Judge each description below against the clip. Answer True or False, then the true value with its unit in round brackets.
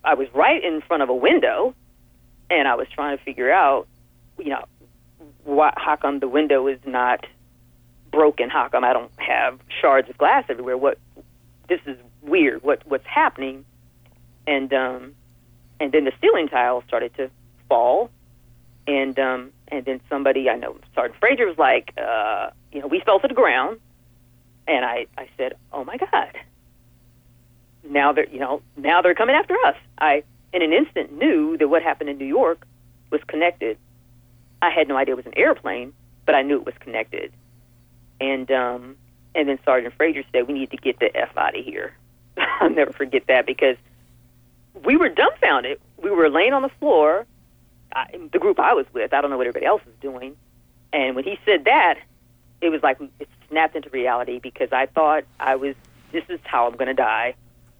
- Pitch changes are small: False (4.0 semitones)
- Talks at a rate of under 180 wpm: False (185 wpm)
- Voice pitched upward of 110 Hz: True (130 Hz)